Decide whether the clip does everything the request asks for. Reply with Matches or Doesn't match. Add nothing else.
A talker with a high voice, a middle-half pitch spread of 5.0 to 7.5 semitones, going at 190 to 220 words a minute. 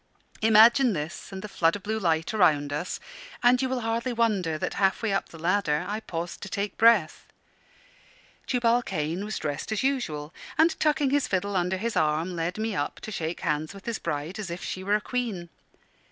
Matches